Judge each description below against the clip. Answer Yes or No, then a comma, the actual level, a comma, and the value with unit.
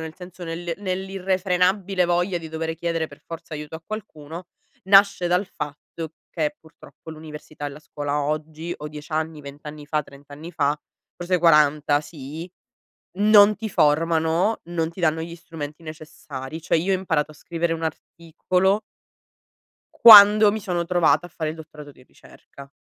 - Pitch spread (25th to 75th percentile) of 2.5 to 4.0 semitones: Yes, average, 2.9 semitones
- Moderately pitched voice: Yes, medium, 165 Hz